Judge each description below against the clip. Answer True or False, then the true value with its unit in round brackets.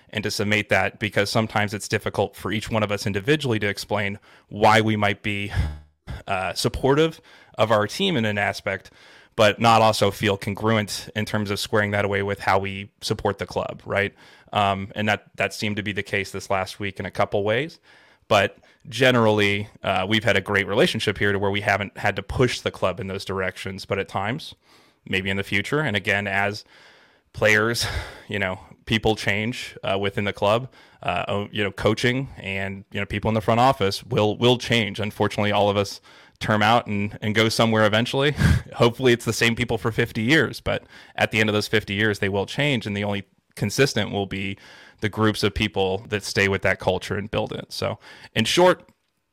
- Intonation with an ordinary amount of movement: False (2.0 semitones)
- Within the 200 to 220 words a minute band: True (205 wpm)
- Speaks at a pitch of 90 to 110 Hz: True (105 Hz)